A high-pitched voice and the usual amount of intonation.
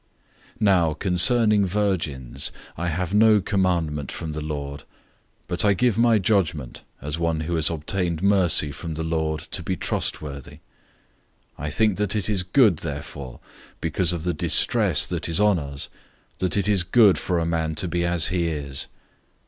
No: very low, 85 Hz; average, 4.3 semitones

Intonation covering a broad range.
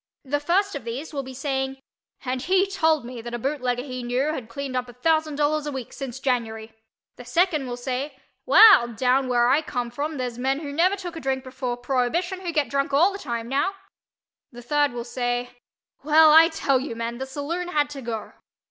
No: average, 3.8 semitones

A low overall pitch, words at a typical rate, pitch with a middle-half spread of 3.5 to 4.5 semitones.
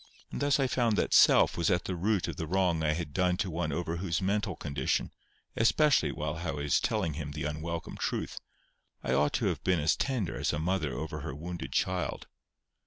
No: very low, 85 Hz; fast, 210 wpm; average, 4.0 semitones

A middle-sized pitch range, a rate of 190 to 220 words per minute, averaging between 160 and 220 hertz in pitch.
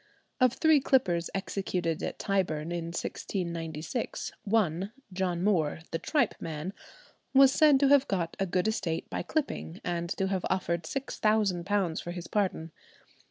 No: average, 4.2 semitones; average, 145 wpm; medium, 185 Hz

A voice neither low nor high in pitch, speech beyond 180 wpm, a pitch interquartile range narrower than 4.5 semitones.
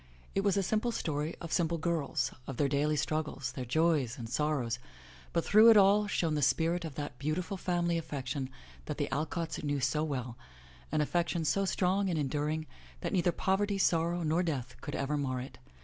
Yes: medium, 155 Hz; average, 195 wpm; average, 3.8 semitones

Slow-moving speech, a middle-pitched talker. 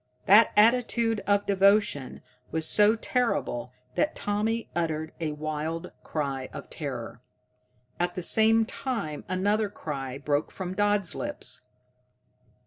No: slow, 120 wpm; high, 195 Hz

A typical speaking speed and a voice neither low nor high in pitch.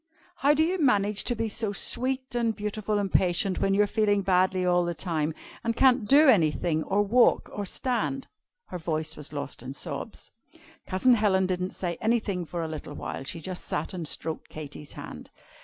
No: average, 190 wpm; high, 195 Hz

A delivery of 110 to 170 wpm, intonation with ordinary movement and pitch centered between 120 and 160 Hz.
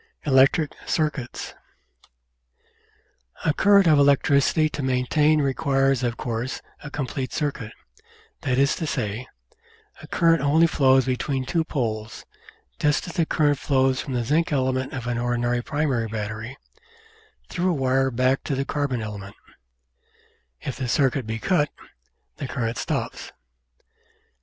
Yes: average, 140 wpm; average, 3.3 semitones; low, 135 Hz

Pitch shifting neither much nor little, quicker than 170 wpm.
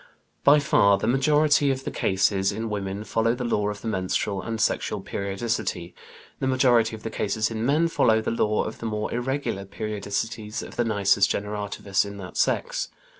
Yes: average, 3.0 semitones; average, 180 wpm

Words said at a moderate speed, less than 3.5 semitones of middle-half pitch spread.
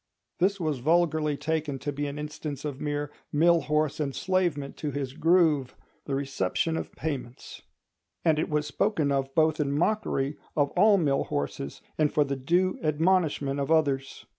Yes: average, 160 wpm; narrow, 2.6 semitones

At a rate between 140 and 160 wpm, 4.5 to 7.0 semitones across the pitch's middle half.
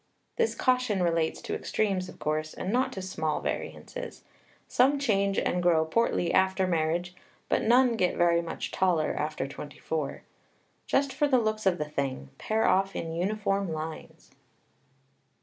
Yes: average, 155 wpm; average, 5.2 semitones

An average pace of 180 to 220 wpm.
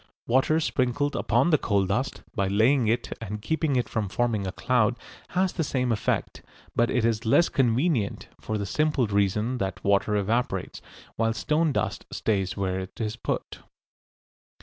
No: average, 165 wpm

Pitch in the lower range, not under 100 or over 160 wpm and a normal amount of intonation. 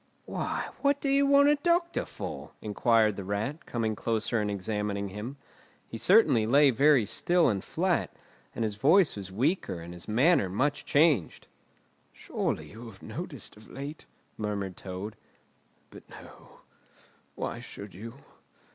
No: low, 115 Hz; average, 145 wpm; wide, 6.7 semitones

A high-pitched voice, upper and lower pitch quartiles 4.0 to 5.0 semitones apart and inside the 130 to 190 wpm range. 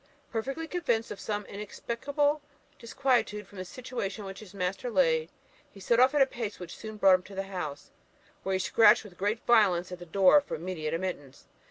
No: high, 205 Hz; average, 4.3 semitones; average, 200 wpm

